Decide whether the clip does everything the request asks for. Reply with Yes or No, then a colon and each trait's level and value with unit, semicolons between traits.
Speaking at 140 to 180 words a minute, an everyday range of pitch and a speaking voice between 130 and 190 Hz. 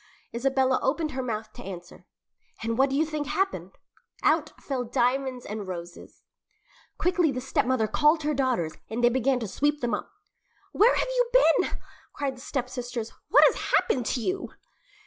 No: average, 165 wpm; average, 4.1 semitones; very high, 260 Hz